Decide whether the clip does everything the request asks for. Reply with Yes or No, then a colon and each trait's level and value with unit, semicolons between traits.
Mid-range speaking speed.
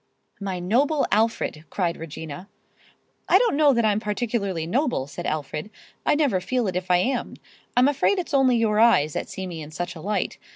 Yes: average, 195 wpm